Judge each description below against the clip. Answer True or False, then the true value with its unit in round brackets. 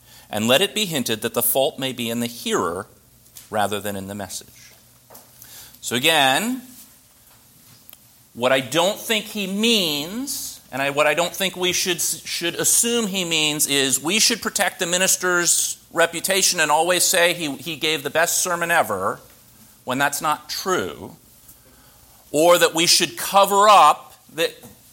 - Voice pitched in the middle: True (165 Hz)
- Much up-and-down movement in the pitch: True (6.9 semitones)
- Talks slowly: False (160 wpm)